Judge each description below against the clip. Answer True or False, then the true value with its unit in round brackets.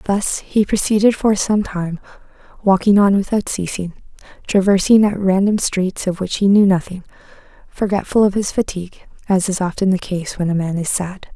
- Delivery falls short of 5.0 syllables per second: False (5.1 syllables/s)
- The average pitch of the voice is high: True (195 Hz)